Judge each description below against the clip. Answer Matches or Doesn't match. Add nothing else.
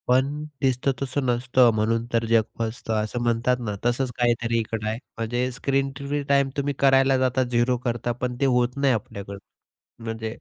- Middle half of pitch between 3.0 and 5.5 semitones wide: Doesn't match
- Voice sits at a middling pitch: Doesn't match